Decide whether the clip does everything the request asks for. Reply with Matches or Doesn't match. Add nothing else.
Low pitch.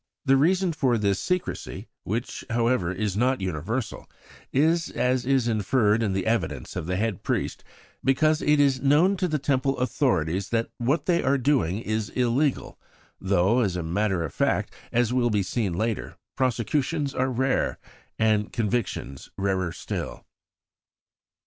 Matches